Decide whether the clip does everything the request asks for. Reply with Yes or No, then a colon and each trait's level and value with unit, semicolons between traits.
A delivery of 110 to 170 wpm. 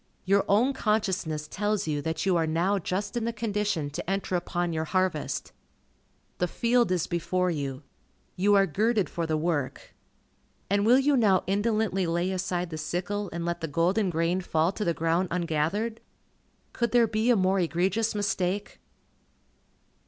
Yes: average, 165 wpm